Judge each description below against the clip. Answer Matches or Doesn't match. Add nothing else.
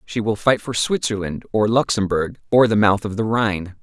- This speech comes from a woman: Doesn't match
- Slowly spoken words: Doesn't match